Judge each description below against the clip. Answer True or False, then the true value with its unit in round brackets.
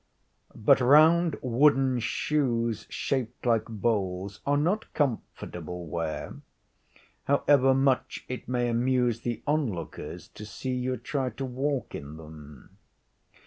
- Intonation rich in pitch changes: False (4.2 semitones)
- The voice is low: True (125 Hz)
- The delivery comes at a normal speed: False (115 wpm)